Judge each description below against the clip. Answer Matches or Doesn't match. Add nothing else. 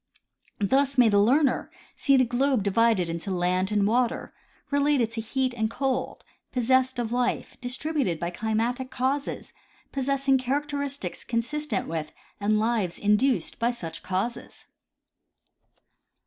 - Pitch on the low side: Doesn't match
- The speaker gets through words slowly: Matches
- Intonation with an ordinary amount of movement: Matches